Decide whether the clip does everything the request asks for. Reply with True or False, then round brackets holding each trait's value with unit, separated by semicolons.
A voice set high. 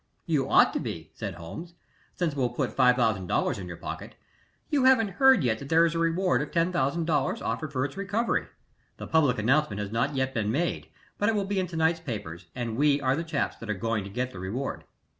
False (140 Hz)